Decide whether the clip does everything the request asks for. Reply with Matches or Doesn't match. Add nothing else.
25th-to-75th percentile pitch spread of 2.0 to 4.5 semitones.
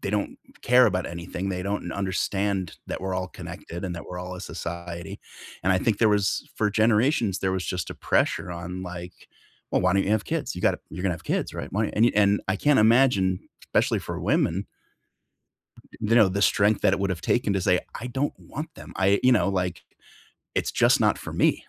Matches